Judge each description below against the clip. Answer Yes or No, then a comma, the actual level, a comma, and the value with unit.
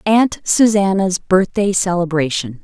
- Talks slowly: Yes, slow, 90 wpm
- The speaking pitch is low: No, high, 190 Hz